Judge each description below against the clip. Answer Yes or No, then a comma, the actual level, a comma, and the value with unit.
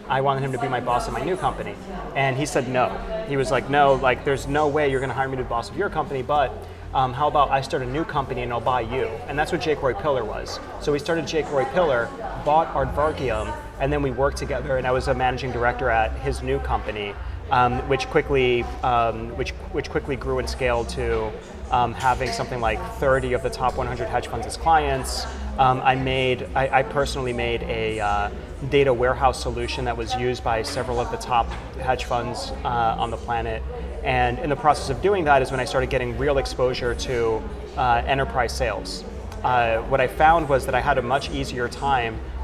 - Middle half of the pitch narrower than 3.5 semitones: Yes, narrow, 2.5 semitones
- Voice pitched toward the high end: No, low, 130 Hz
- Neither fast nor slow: No, fast, 220 wpm